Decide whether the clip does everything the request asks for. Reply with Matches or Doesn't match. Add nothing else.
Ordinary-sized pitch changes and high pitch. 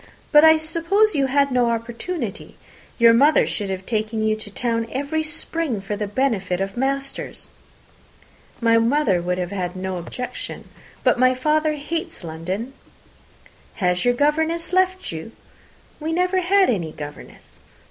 Doesn't match